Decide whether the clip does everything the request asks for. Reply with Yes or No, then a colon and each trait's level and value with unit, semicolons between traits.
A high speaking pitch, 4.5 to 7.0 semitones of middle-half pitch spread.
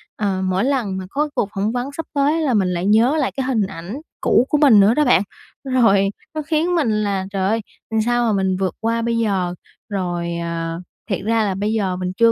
Yes: high, 215 Hz; average, 5.1 semitones